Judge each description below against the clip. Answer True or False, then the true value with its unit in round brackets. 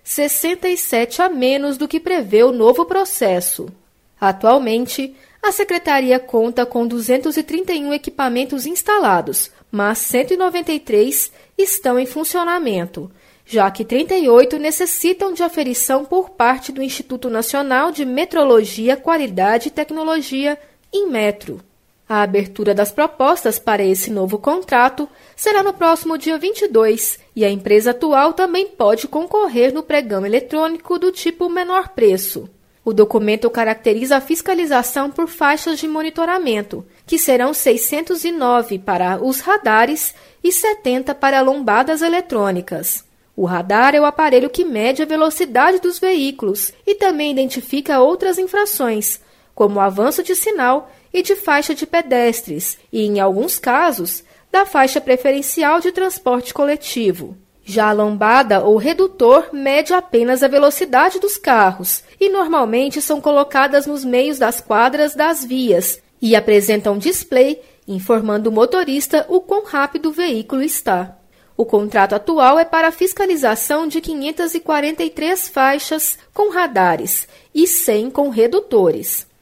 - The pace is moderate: True (130 wpm)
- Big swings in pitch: True (6.3 semitones)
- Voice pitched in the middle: False (280 Hz)